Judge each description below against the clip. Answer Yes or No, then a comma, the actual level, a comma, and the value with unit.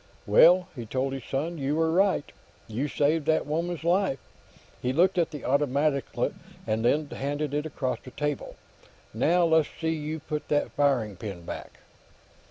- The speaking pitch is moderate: Yes, medium, 145 Hz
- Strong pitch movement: No, average, 3.4 semitones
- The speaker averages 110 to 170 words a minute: Yes, average, 165 wpm